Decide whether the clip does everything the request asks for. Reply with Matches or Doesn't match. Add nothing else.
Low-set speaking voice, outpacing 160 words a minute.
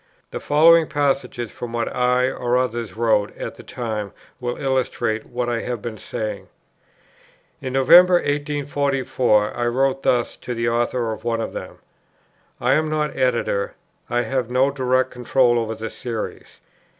Doesn't match